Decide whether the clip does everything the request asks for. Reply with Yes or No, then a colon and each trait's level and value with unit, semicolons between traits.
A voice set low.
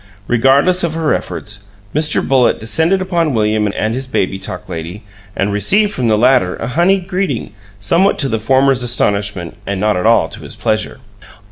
Yes: low, 120 Hz